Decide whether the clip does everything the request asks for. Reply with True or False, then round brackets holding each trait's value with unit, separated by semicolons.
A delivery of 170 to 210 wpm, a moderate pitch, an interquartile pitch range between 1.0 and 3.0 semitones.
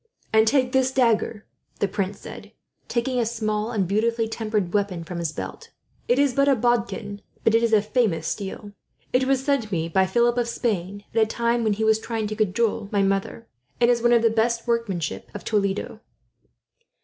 False (195 wpm; 220 Hz; 2.7 semitones)